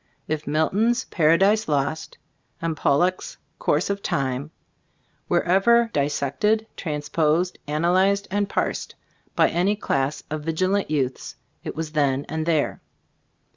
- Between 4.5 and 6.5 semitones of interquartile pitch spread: Yes, average, 4.8 semitones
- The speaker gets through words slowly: Yes, slow, 125 wpm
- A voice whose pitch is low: No, medium, 160 Hz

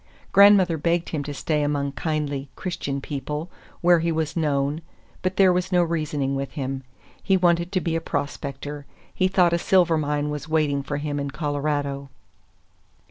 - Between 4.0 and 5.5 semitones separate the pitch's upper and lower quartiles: No, average, 3.2 semitones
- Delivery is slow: No, average, 170 wpm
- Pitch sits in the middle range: Yes, medium, 150 Hz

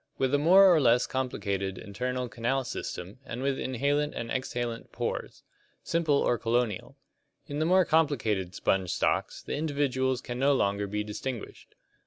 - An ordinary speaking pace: Yes, average, 155 wpm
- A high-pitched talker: No, low, 125 Hz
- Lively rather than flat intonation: No, average, 4.1 semitones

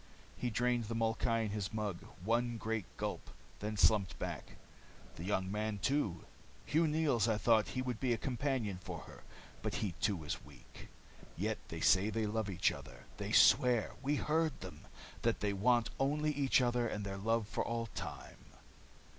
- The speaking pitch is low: Yes, low, 110 Hz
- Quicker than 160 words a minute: Yes, average, 180 wpm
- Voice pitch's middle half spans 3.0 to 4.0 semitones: Yes, average, 3.5 semitones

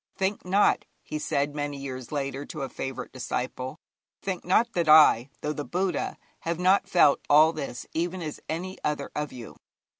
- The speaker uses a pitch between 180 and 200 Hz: No, medium, 150 Hz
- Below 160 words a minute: No, average, 175 wpm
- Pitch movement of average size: Yes, average, 4.3 semitones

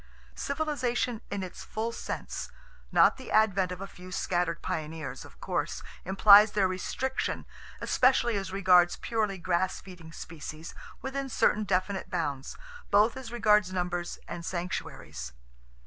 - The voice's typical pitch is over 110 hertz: Yes, high, 190 Hz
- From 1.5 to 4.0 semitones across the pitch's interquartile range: Yes, average, 3.7 semitones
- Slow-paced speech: Yes, slow, 125 wpm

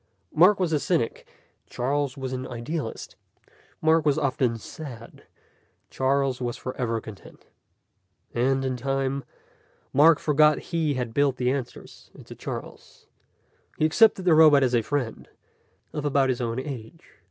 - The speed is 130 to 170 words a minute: Yes, average, 140 wpm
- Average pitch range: Yes, average, 3.4 semitones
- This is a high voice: No, low, 135 Hz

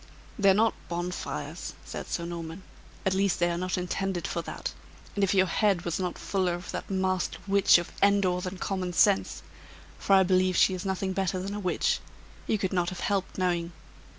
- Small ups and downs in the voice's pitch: Yes, narrow, 1.6 semitones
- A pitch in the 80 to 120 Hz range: No, medium, 185 Hz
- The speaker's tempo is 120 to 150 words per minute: No, average, 195 wpm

